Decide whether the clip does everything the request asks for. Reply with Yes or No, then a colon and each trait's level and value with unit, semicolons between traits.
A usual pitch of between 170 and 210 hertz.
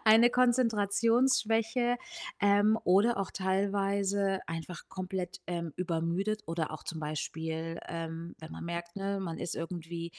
Yes: high, 190 Hz